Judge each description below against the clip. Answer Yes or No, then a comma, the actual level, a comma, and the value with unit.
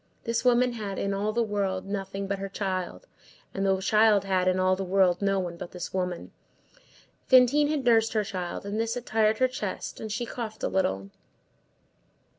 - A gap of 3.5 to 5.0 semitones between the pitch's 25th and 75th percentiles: No, average, 3.0 semitones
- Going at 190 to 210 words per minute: Yes, average, 195 wpm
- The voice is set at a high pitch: Yes, high, 200 Hz